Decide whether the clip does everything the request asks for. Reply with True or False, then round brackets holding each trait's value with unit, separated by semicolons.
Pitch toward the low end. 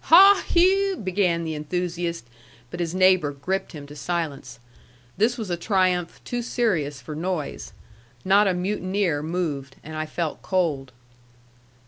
False (175 Hz)